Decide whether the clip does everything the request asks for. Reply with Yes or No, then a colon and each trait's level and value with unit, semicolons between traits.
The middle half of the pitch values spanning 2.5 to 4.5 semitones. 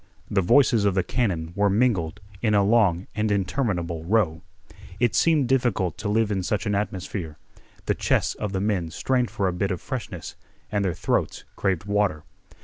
Yes: average, 3.5 semitones